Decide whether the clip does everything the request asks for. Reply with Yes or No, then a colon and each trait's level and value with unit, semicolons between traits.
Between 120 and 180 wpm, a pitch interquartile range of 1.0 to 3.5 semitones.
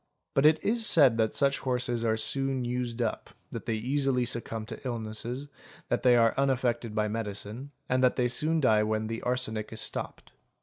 No: average, 190 wpm; average, 3.0 semitones